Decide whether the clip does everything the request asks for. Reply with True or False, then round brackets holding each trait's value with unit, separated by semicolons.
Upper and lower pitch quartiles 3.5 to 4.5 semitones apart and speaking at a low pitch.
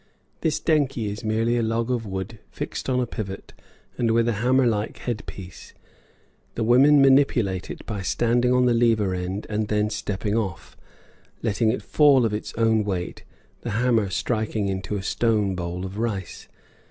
False (3.1 semitones; 110 Hz)